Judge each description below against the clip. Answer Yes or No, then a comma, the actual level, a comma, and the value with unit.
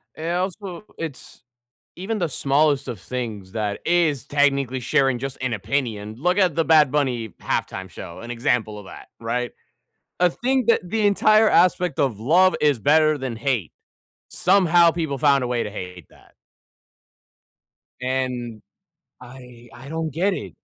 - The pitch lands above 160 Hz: No, low, 135 Hz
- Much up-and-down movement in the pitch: Yes, wide, 5.9 semitones